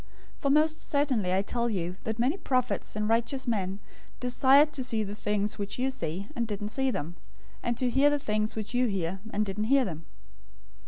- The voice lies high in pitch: Yes, high, 225 Hz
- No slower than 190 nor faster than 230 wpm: Yes, fast, 205 wpm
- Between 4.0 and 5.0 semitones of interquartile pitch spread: Yes, average, 4.5 semitones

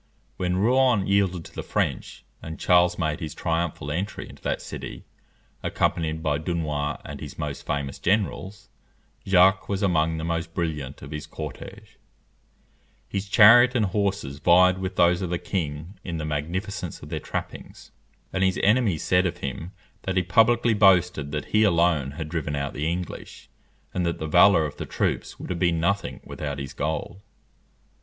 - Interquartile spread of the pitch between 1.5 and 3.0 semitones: No, average, 3.9 semitones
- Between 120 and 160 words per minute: No, average, 170 wpm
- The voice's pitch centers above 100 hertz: No, very low, 85 Hz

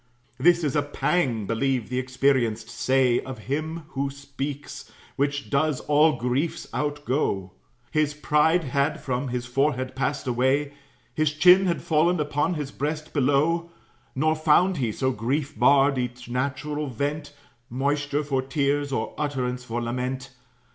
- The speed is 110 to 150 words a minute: Yes, average, 140 wpm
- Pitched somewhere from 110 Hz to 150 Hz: Yes, medium, 140 Hz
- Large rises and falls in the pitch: No, average, 2.7 semitones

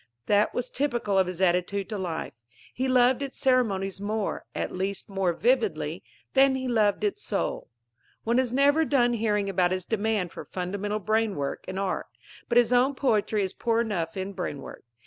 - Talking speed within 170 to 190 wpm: Yes, average, 175 wpm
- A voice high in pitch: Yes, high, 210 Hz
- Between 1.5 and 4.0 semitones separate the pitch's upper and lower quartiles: No, average, 4.6 semitones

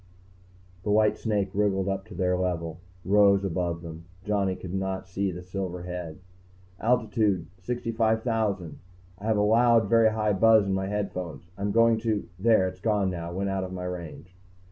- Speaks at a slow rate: No, average, 170 wpm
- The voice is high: No, very low, 95 Hz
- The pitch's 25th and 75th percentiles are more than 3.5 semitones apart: No, average, 3.0 semitones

